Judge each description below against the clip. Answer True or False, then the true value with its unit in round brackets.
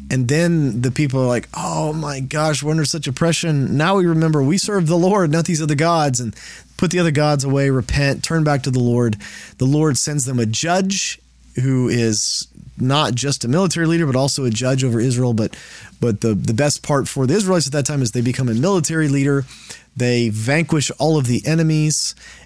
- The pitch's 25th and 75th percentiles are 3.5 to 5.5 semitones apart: True (4.2 semitones)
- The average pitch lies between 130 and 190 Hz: True (140 Hz)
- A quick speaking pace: True (210 wpm)